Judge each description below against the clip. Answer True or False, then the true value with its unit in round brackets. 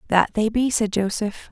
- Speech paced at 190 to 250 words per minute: True (200 wpm)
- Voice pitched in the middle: False (215 Hz)